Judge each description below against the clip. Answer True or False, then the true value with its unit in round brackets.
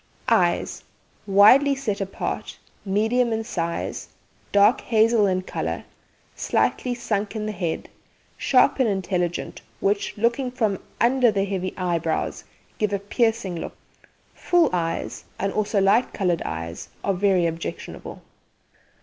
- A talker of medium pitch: False (200 Hz)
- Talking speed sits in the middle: False (125 wpm)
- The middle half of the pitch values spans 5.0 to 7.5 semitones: False (3.8 semitones)